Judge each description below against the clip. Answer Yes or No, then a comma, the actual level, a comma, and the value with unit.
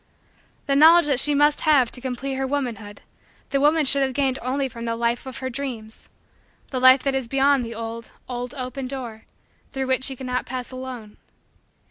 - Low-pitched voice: No, very high, 260 Hz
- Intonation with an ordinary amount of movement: No, narrow, 2.3 semitones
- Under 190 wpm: No, average, 195 wpm